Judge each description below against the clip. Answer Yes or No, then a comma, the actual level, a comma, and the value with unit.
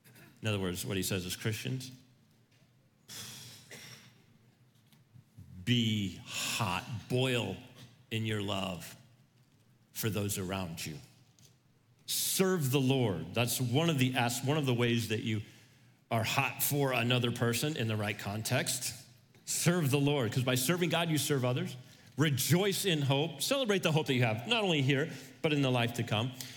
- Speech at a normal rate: Yes, average, 155 wpm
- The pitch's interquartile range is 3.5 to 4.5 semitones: No, average, 2.9 semitones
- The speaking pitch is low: Yes, low, 125 Hz